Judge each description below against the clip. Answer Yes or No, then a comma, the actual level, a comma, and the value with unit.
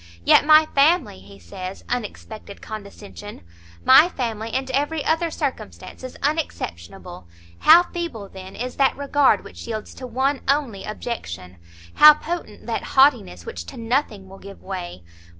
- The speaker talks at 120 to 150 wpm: Yes, average, 145 wpm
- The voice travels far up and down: Yes, wide, 6.9 semitones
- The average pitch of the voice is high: Yes, high, 235 Hz